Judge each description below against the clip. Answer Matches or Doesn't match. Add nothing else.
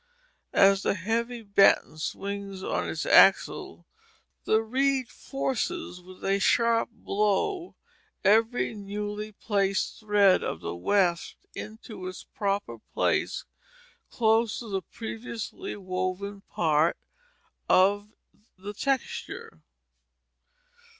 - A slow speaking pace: Matches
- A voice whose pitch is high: Matches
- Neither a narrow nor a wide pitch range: Matches